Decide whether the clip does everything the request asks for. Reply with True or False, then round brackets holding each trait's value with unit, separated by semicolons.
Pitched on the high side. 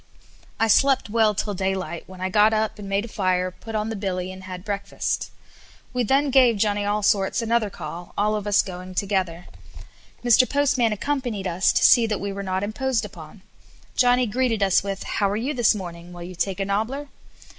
True (205 Hz)